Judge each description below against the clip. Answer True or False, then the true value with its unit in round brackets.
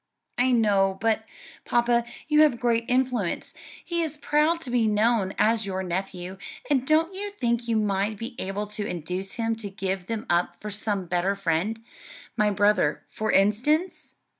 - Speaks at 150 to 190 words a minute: True (165 wpm)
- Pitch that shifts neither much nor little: True (3.8 semitones)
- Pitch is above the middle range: True (220 Hz)